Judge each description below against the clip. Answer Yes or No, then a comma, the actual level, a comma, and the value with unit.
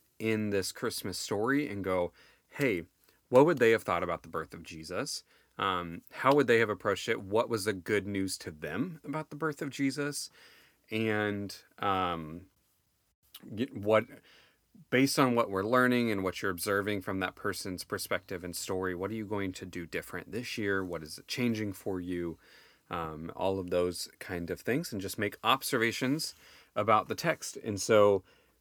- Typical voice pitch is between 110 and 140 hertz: No, low, 100 Hz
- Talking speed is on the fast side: No, average, 180 wpm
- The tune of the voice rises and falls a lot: No, average, 3.8 semitones